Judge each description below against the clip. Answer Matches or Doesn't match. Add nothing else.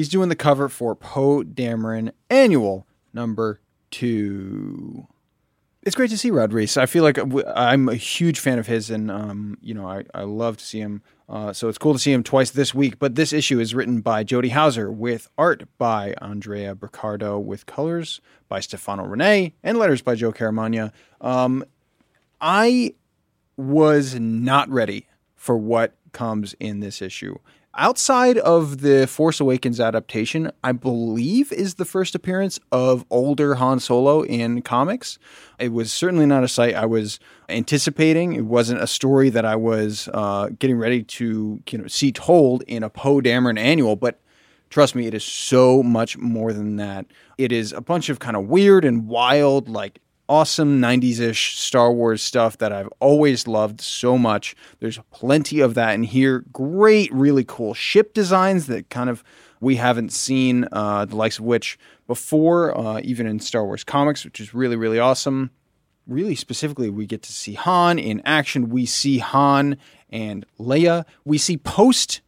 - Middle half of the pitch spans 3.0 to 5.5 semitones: Matches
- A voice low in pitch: Matches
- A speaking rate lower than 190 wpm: Matches